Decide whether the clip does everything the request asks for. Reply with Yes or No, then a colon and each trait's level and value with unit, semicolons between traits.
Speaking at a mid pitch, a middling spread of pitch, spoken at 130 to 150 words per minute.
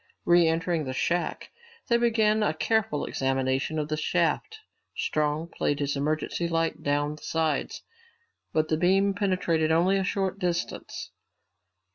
Yes: medium, 165 Hz; average, 3.9 semitones; average, 140 wpm